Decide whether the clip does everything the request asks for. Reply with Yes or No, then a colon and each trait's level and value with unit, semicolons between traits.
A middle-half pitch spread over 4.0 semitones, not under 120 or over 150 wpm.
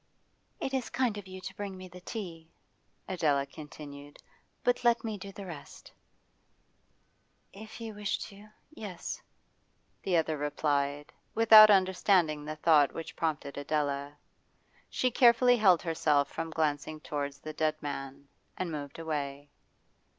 Yes: wide, 5.5 semitones; slow, 135 wpm